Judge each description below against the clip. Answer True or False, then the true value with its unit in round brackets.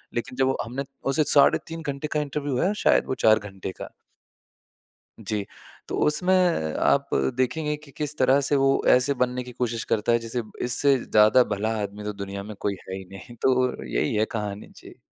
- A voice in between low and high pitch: False (125 Hz)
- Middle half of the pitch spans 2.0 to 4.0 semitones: False (4.6 semitones)